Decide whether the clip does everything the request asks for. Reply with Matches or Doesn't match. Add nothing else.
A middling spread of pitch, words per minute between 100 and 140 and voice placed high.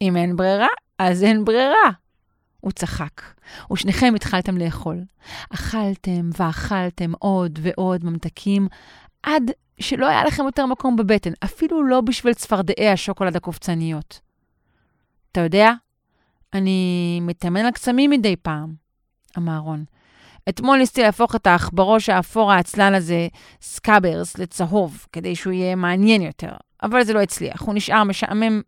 Matches